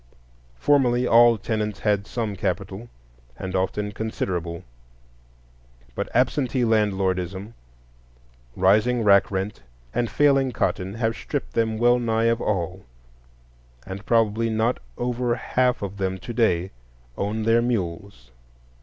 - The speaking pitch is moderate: No, low, 110 Hz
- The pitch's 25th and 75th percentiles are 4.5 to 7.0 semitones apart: No, average, 3.7 semitones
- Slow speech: Yes, slow, 120 wpm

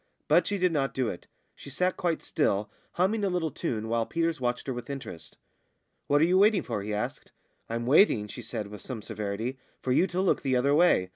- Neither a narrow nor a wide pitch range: No, wide, 7.4 semitones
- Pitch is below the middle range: Yes, low, 130 Hz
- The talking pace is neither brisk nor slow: No, fast, 220 wpm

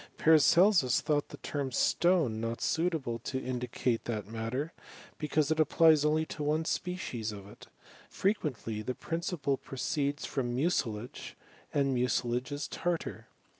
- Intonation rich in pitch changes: No, average, 4.8 semitones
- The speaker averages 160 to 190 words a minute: No, slow, 135 wpm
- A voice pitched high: No, medium, 140 Hz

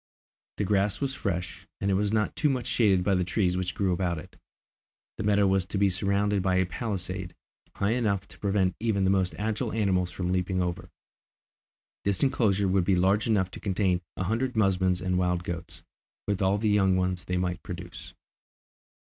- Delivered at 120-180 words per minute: No, average, 190 wpm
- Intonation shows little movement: Yes, narrow, 2.1 semitones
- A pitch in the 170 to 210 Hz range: No, very low, 95 Hz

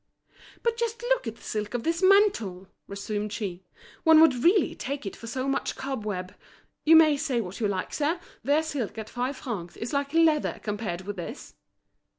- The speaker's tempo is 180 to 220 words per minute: Yes, average, 185 wpm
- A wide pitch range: Yes, wide, 7.2 semitones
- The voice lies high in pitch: Yes, very high, 250 Hz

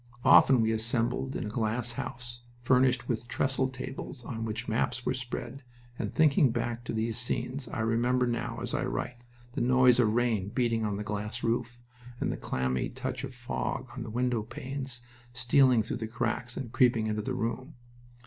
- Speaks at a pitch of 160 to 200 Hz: No, low, 120 Hz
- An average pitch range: No, narrow, 2.0 semitones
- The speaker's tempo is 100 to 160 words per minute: No, average, 185 wpm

